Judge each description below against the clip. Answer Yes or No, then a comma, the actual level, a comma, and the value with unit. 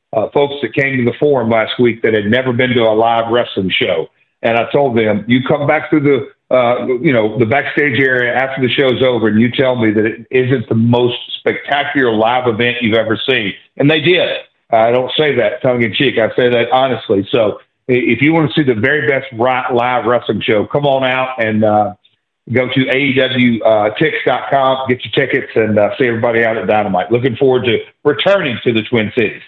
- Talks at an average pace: No, fast, 210 wpm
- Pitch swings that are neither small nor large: Yes, average, 3.0 semitones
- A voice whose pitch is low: Yes, low, 125 Hz